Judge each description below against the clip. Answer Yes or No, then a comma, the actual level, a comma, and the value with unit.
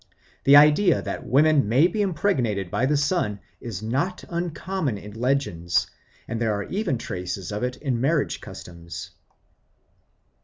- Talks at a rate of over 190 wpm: No, average, 145 wpm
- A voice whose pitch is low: Yes, low, 130 Hz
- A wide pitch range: Yes, wide, 7.2 semitones